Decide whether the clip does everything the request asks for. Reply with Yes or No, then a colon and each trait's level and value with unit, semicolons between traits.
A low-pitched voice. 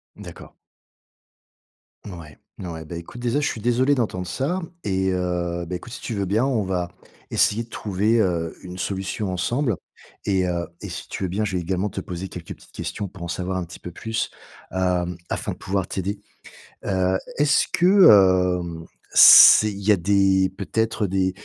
Yes: very low, 95 Hz